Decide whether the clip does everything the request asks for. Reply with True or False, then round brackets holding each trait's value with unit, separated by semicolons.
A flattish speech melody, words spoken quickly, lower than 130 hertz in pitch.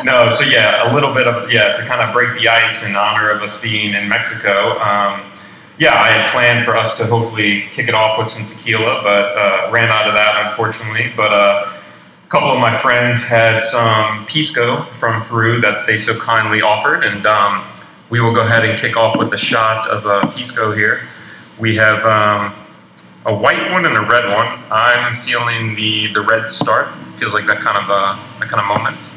True (1.8 semitones; 210 wpm; 110 Hz)